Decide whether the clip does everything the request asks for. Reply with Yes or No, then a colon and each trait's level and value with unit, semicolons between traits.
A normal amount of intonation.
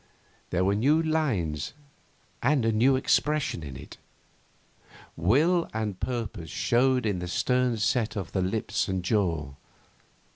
No: wide, 6.3 semitones